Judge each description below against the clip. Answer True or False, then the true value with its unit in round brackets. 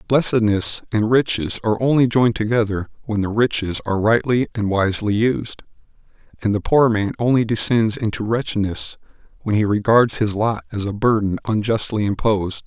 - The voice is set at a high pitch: False (110 Hz)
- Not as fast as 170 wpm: True (155 wpm)